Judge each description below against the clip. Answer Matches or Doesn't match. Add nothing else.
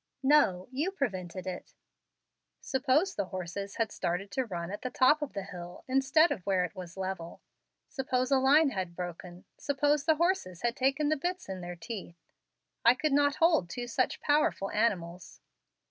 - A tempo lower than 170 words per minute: Doesn't match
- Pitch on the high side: Matches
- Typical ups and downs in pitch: Doesn't match